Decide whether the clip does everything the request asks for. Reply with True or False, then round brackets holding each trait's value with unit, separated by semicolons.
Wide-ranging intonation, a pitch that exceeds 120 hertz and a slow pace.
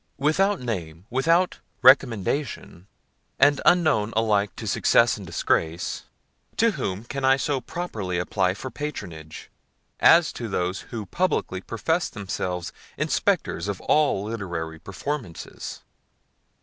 False (7.7 semitones; 110 Hz; 115 wpm)